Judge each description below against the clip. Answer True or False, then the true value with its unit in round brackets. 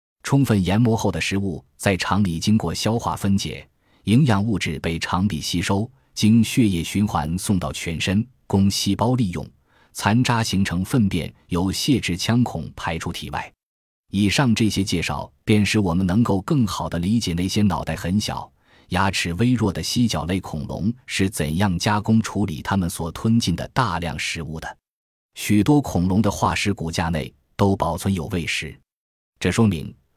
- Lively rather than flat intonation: False (4.4 semitones)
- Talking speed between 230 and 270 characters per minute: True (250 characters per minute)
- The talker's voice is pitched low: True (100 Hz)